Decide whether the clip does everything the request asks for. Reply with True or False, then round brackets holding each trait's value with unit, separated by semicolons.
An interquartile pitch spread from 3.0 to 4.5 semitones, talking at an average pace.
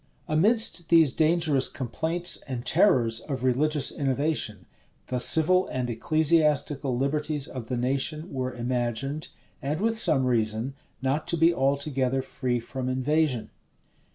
False (3.7 semitones; 125 wpm)